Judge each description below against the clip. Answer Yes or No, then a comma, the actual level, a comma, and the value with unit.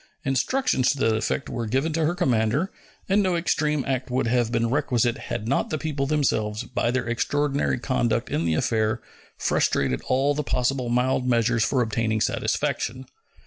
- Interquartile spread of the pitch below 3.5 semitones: No, average, 3.8 semitones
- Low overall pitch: Yes, low, 125 Hz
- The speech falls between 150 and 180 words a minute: Yes, average, 170 wpm